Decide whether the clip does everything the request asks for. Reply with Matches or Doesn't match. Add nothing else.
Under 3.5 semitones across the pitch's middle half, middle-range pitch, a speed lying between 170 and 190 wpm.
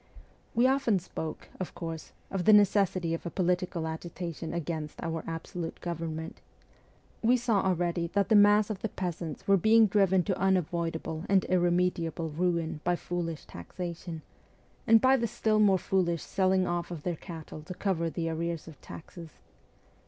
Doesn't match